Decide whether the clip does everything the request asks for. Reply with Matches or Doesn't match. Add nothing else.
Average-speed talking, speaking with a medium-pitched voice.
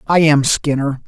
Matches